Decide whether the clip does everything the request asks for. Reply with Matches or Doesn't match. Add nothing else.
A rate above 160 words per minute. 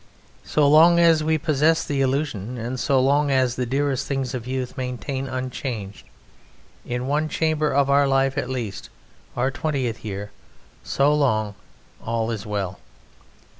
Doesn't match